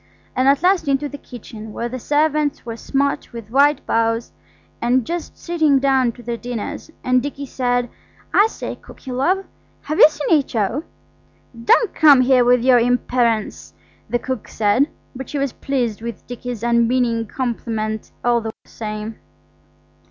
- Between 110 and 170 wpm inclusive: Yes, average, 155 wpm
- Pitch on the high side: Yes, very high, 250 Hz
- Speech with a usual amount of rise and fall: Yes, average, 3.3 semitones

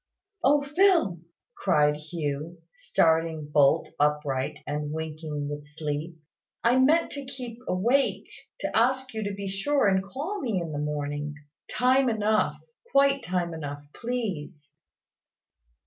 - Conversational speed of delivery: No, slow, 130 wpm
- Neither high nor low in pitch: Yes, medium, 175 Hz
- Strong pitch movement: Yes, wide, 9.0 semitones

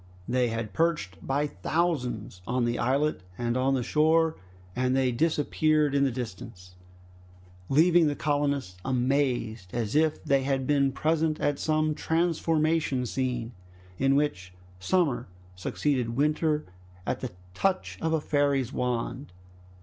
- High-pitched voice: No, medium, 140 Hz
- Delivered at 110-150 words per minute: Yes, slow, 135 wpm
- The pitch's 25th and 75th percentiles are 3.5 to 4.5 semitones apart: Yes, average, 4.0 semitones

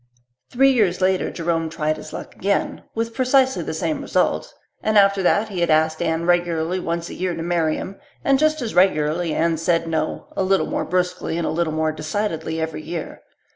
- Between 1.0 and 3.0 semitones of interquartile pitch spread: No, average, 3.5 semitones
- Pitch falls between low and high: Yes, medium, 175 Hz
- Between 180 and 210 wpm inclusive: Yes, average, 200 wpm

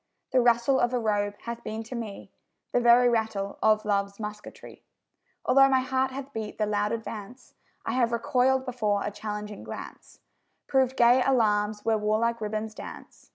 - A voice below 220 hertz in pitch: No, high, 225 Hz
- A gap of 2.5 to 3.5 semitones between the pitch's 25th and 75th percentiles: Yes, average, 2.9 semitones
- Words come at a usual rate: Yes, average, 165 wpm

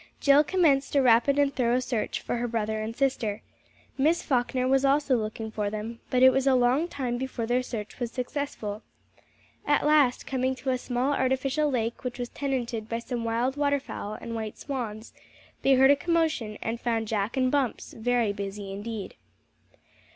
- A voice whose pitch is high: Yes, very high, 250 Hz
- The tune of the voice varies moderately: Yes, average, 3.3 semitones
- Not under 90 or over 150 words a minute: No, average, 180 wpm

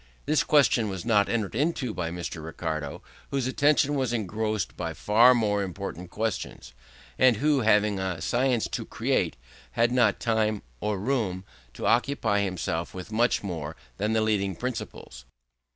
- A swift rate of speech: No, average, 150 wpm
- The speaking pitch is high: No, low, 105 Hz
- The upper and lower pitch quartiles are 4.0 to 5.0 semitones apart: Yes, average, 4.6 semitones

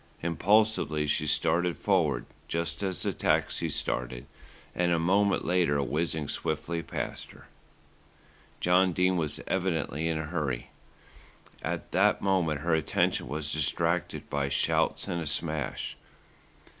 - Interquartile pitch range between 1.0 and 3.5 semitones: Yes, average, 3.0 semitones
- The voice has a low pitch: Yes, very low, 85 Hz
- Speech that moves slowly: Yes, slow, 130 wpm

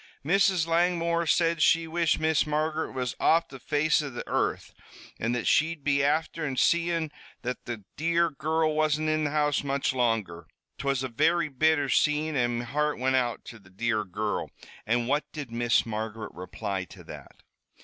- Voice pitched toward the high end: No, medium, 145 Hz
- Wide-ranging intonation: No, average, 4.7 semitones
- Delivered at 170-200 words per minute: Yes, average, 180 wpm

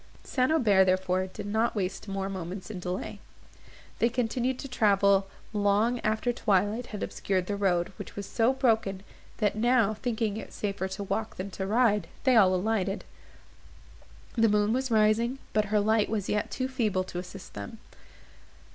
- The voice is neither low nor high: No, high, 210 Hz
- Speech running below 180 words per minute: Yes, average, 165 wpm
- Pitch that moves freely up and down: No, average, 2.9 semitones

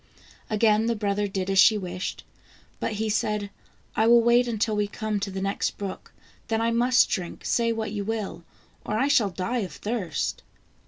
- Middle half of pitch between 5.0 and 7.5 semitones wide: No, narrow, 2.5 semitones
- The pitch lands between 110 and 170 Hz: No, high, 210 Hz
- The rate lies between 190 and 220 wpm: Yes, average, 195 wpm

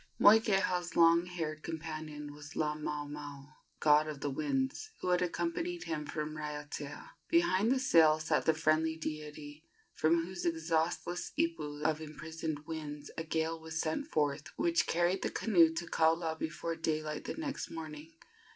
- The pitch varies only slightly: Yes, narrow, 2.1 semitones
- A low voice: No, medium, 160 Hz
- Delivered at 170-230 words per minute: No, average, 150 wpm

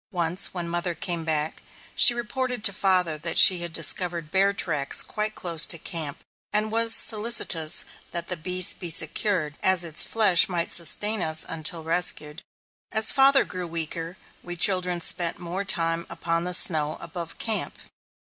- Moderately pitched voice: Yes, medium, 175 Hz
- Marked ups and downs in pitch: No, average, 3.0 semitones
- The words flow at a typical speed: Yes, average, 160 wpm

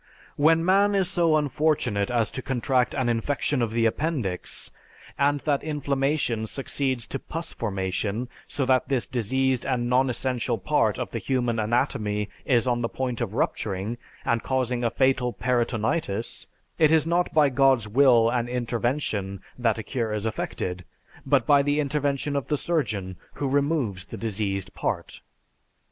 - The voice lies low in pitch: Yes, low, 125 Hz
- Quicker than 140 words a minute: Yes, average, 155 wpm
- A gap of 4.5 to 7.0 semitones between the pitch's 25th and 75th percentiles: No, average, 3.9 semitones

